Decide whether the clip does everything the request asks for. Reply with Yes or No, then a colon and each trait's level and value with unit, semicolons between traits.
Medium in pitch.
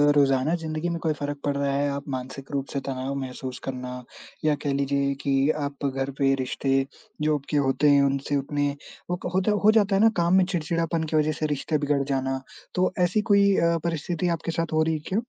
Yes: medium, 145 Hz